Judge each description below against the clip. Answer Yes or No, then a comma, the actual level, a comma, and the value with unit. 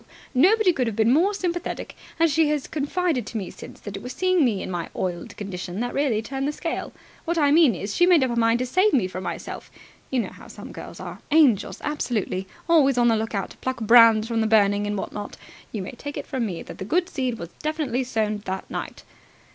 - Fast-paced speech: Yes, fast, 240 wpm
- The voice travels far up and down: Yes, wide, 6.4 semitones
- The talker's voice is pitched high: Yes, high, 245 Hz